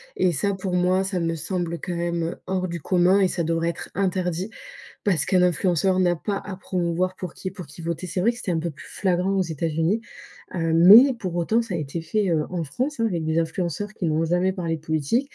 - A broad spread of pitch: No, narrow, 2.4 semitones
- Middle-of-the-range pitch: Yes, medium, 180 Hz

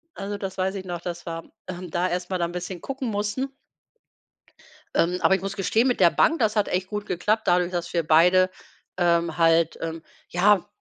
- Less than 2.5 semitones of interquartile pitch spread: No, average, 2.8 semitones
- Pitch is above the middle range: No, medium, 180 Hz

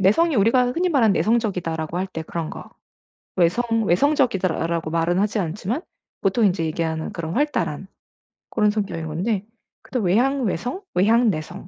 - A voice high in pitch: Yes, high, 200 Hz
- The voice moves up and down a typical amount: No, wide, 6.0 semitones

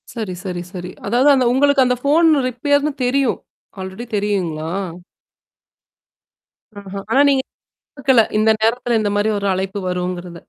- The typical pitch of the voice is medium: No, high, 220 Hz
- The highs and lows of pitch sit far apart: Yes, wide, 5.9 semitones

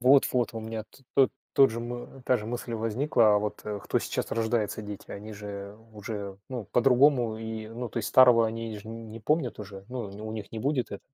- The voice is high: No, low, 115 Hz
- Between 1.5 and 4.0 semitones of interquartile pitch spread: Yes, narrow, 2.6 semitones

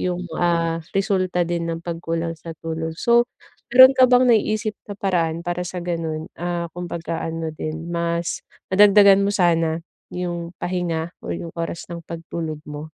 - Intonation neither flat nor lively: No, narrow, 1.8 semitones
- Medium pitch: Yes, medium, 170 Hz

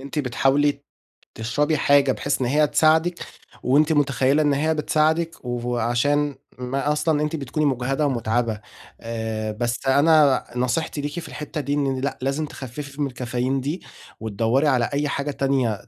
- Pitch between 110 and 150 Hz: Yes, medium, 140 Hz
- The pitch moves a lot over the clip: No, average, 3.2 semitones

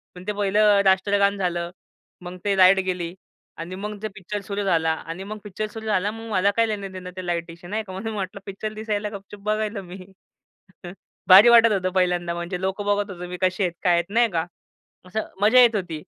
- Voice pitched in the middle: No, high, 195 Hz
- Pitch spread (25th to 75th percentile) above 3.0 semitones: No, average, 2.7 semitones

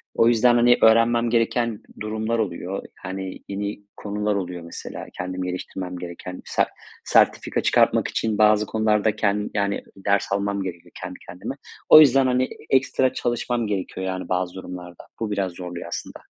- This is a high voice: No, low, 100 Hz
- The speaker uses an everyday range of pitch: Yes, average, 3.7 semitones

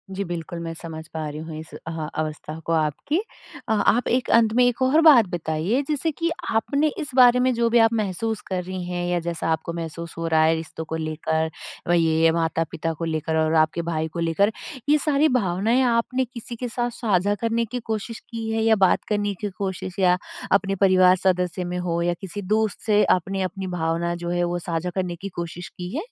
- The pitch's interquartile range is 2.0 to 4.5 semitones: No, wide, 5.4 semitones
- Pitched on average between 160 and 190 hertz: Yes, medium, 185 Hz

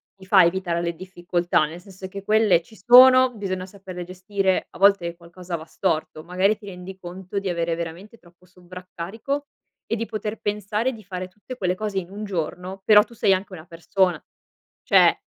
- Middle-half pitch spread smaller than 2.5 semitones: No, average, 2.8 semitones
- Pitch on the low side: No, medium, 185 Hz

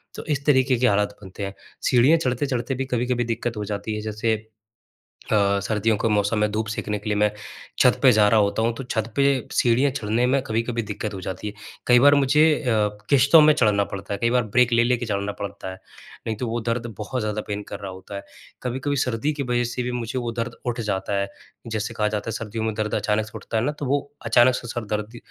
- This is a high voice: No, low, 115 Hz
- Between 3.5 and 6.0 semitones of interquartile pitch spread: No, average, 2.9 semitones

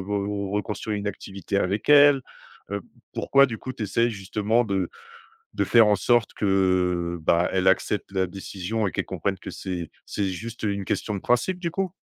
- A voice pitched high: No, low, 100 Hz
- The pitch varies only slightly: No, average, 3.2 semitones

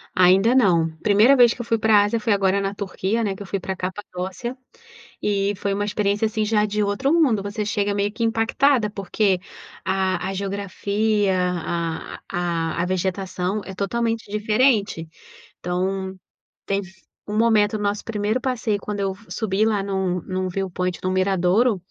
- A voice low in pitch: No, high, 200 Hz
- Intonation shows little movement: Yes, narrow, 2.3 semitones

